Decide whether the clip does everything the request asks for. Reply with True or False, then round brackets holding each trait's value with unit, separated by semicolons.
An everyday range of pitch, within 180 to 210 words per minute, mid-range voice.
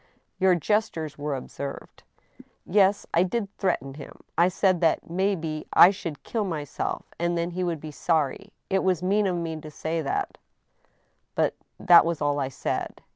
True (3.6 semitones; 185 wpm; 170 Hz)